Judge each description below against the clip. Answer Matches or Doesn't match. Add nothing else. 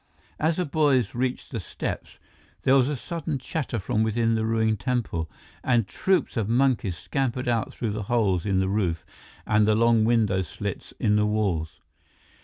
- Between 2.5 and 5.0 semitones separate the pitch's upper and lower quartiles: Matches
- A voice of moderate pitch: Doesn't match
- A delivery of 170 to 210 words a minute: Matches